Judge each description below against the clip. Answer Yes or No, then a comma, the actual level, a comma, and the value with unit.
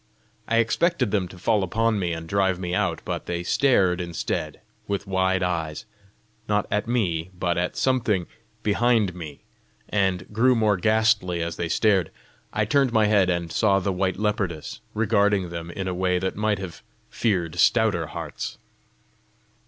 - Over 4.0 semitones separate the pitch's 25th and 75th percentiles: No, average, 3.5 semitones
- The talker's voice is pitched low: Yes, very low, 95 Hz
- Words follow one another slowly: No, average, 160 wpm